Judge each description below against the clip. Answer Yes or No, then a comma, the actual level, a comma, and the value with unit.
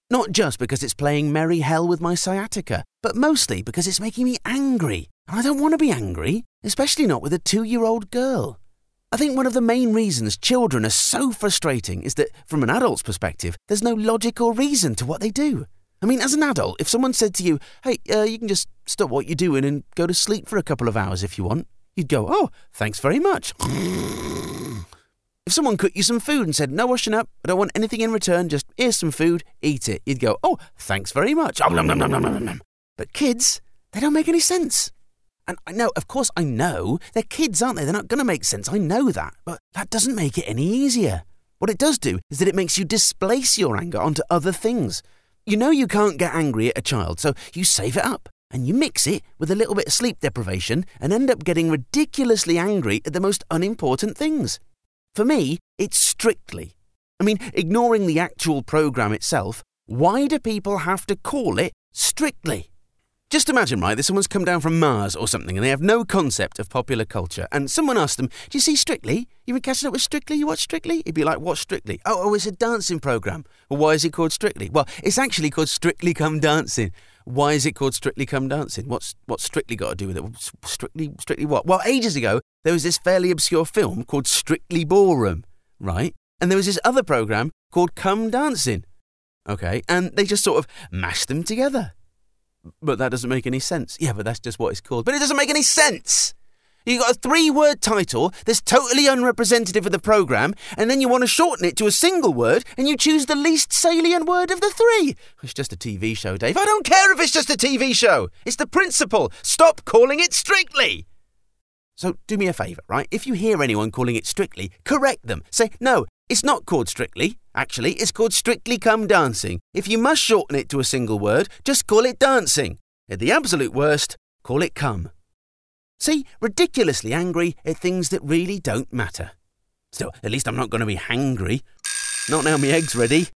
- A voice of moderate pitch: Yes, medium, 180 Hz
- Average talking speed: No, fast, 220 wpm